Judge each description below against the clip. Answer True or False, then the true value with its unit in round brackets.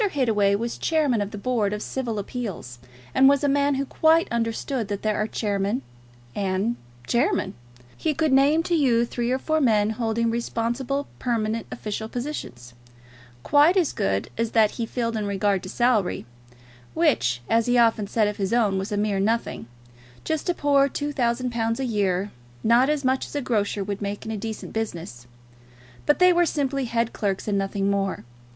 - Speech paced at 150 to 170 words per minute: False (185 wpm)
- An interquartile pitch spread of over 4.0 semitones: True (4.6 semitones)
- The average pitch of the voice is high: True (230 Hz)